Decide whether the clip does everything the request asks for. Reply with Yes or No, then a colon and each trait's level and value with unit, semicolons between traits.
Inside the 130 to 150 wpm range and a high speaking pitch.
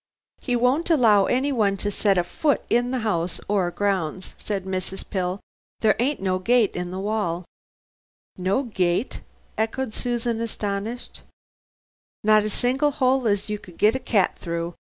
No: average, 160 wpm; high, 210 Hz